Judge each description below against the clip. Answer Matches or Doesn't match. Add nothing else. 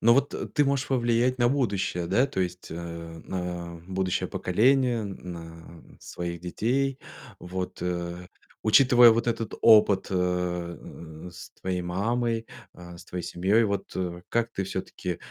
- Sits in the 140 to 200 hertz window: Doesn't match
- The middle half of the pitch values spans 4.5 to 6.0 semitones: Matches